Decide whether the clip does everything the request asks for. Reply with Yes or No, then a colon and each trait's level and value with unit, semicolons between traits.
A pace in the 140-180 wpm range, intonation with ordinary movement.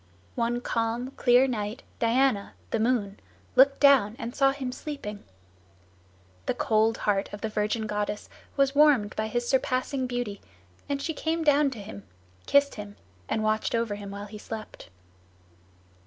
Yes: average, 155 wpm; average, 4.3 semitones